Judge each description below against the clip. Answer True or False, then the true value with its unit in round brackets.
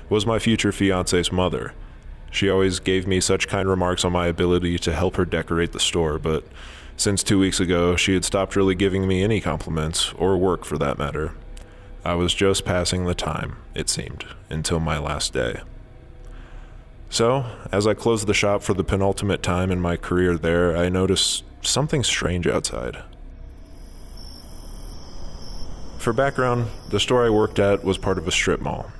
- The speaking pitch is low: True (90 Hz)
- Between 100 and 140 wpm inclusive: False (170 wpm)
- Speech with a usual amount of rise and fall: True (3.3 semitones)